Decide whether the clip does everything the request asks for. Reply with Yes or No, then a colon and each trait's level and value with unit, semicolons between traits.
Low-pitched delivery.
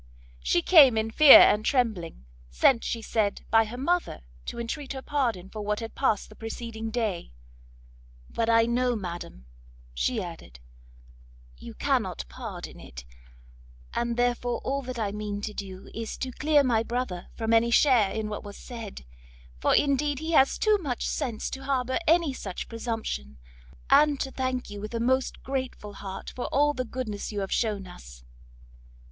No: high, 230 Hz